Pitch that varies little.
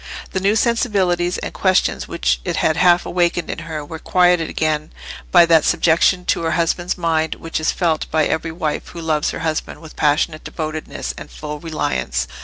Yes: narrow, 2.2 semitones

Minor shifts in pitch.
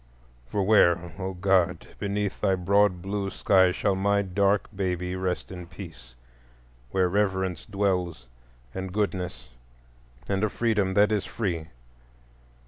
Yes: narrow, 2.3 semitones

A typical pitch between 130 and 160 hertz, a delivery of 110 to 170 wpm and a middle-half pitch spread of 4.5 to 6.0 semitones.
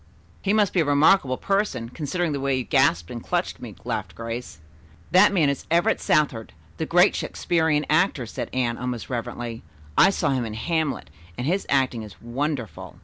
No: medium, 140 Hz; average, 180 wpm; average, 5.2 semitones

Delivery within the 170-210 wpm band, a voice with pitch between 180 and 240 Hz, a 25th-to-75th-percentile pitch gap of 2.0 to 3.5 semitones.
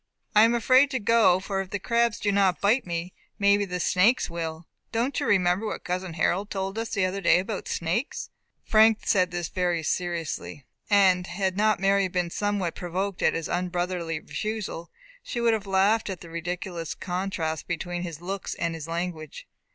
Yes: average, 180 wpm; medium, 185 Hz; average, 2.8 semitones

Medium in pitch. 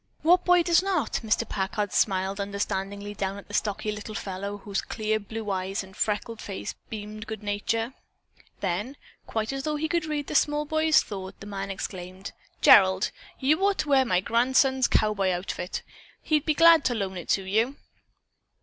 No: high, 215 Hz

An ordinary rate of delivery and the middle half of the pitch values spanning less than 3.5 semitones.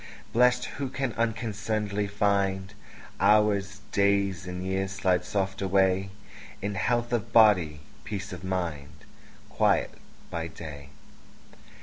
No: slow, 110 wpm; narrow, 2.4 semitones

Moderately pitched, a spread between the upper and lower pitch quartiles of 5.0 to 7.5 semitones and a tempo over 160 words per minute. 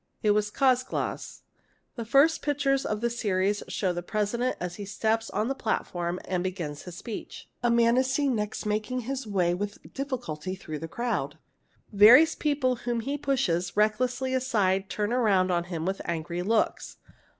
No: high, 215 Hz; average, 5.3 semitones; average, 175 wpm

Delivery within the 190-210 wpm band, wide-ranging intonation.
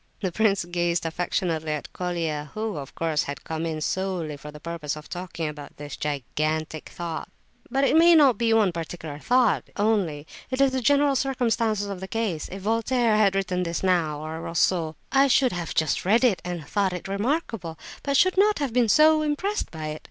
Yes: average, 195 wpm; wide, 6.5 semitones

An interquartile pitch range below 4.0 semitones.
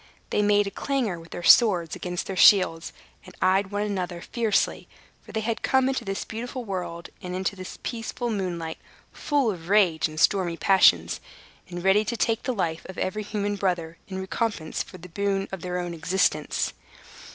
Yes: average, 3.2 semitones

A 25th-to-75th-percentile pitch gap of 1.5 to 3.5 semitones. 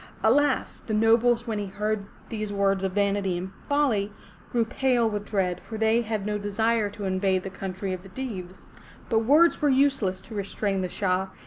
Yes: average, 3.0 semitones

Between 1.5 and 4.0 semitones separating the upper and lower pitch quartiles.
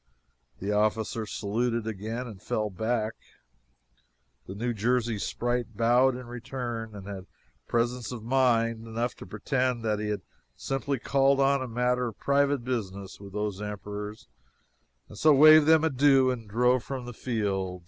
Yes: average, 3.2 semitones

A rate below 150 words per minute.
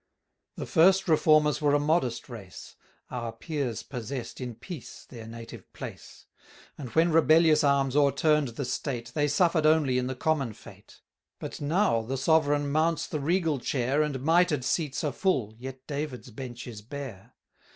No: average, 160 wpm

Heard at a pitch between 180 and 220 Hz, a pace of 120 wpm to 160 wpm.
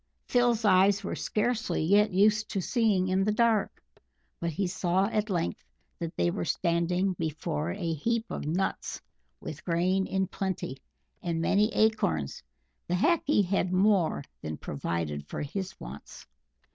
Yes: medium, 185 Hz; average, 145 wpm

